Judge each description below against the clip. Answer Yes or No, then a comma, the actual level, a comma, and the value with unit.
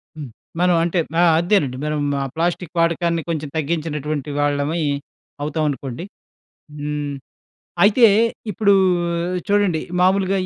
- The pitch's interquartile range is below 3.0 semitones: No, average, 3.3 semitones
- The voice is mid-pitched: Yes, medium, 165 Hz